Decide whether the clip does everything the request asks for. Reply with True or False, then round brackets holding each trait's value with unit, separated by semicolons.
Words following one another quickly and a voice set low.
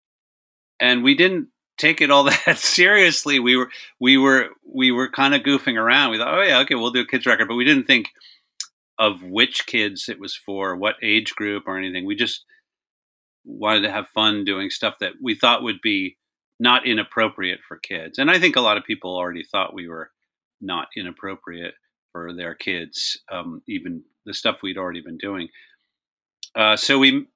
False (190 wpm; 130 Hz)